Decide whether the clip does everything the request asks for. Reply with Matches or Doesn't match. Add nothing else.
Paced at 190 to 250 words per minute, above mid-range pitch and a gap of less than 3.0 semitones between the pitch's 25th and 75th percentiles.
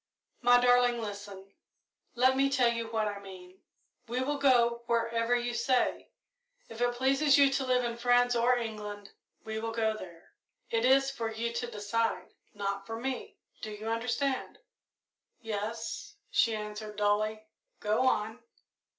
Doesn't match